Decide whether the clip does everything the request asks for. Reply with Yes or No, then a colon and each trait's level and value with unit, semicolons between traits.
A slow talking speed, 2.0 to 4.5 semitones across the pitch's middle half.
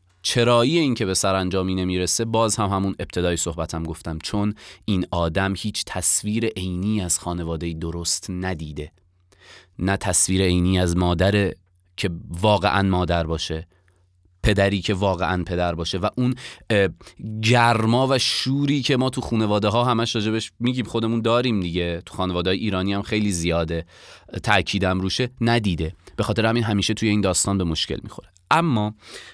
No: average, 150 wpm; average, 3.5 semitones